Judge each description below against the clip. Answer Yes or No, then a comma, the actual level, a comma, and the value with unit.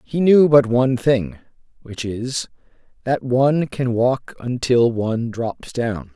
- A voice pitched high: No, low, 125 Hz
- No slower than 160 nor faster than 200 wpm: No, average, 145 wpm